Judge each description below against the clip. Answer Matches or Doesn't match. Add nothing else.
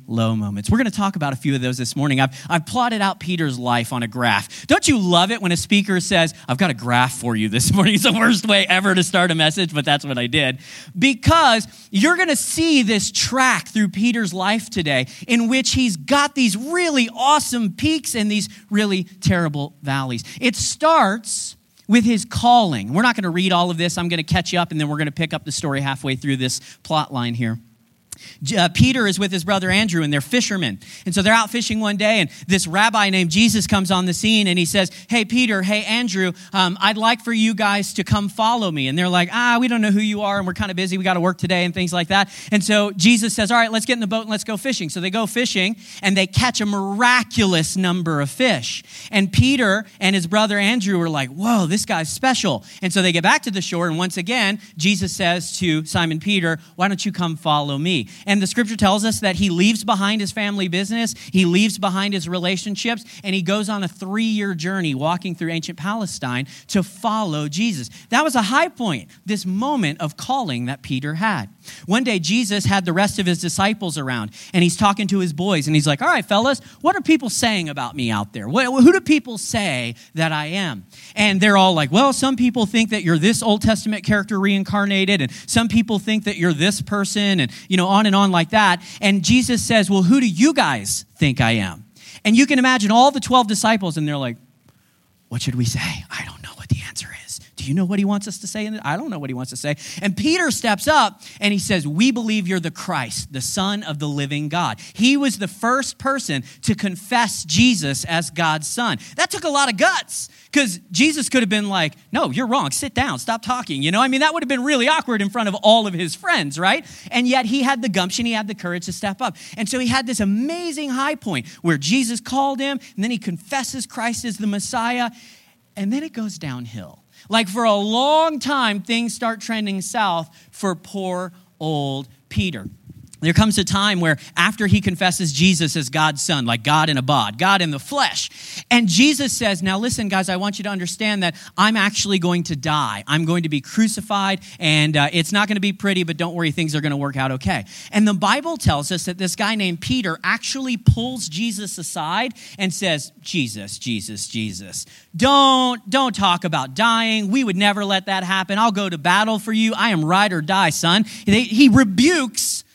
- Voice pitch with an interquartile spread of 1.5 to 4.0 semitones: Doesn't match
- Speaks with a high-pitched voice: Matches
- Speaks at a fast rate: Matches